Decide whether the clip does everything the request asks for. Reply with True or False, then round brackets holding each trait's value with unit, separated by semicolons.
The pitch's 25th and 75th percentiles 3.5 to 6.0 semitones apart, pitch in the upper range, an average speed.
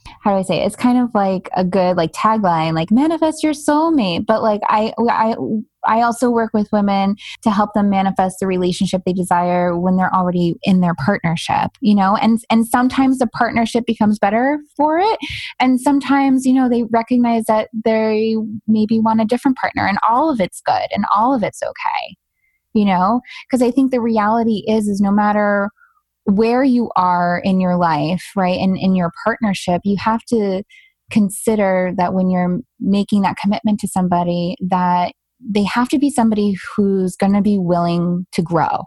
True (4.1 semitones; 210 Hz; 185 wpm)